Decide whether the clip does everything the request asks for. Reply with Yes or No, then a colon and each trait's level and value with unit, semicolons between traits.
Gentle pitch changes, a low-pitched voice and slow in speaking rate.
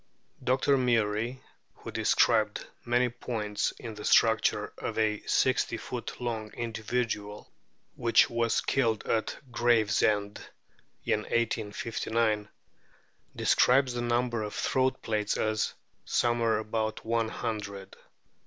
Yes: narrow, 2.0 semitones; low, 115 Hz; slow, 105 wpm